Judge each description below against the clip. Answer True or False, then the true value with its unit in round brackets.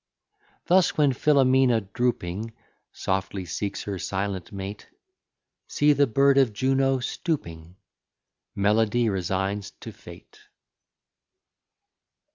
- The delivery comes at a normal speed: False (90 wpm)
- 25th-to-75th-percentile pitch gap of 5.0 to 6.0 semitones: True (5.6 semitones)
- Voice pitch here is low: True (110 Hz)